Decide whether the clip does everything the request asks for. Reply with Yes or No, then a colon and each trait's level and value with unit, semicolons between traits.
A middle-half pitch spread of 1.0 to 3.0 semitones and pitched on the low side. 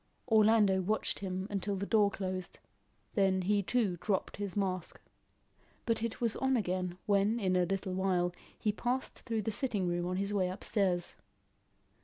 No: narrow, 2.6 semitones; high, 195 Hz